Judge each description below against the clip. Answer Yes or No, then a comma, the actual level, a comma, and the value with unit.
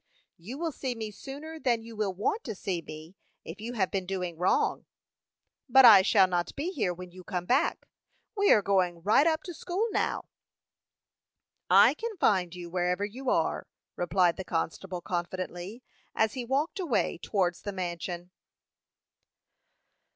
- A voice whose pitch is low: No, high, 195 Hz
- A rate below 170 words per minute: Yes, average, 160 wpm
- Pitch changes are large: Yes, wide, 6.0 semitones